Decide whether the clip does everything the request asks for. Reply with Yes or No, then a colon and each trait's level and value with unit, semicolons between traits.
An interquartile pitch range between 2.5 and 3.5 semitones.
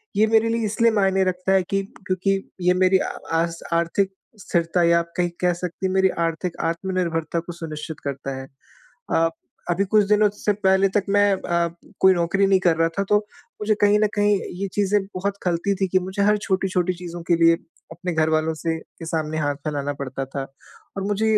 Yes: average, 3.0 semitones